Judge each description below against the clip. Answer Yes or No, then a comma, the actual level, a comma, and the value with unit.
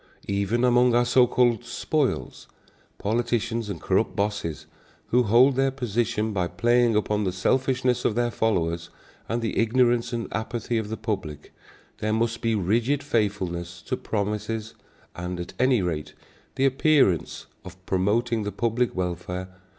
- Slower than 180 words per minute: Yes, average, 145 wpm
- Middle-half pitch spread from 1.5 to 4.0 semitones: Yes, average, 3.7 semitones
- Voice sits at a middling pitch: No, low, 110 Hz